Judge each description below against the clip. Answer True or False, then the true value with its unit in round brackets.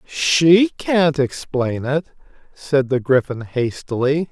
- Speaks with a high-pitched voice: False (145 Hz)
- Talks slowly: True (110 wpm)